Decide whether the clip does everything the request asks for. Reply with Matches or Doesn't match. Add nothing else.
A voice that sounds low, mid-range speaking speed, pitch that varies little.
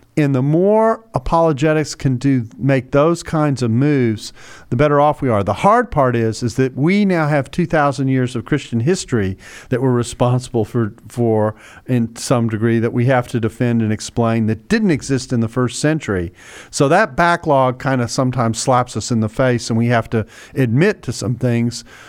Doesn't match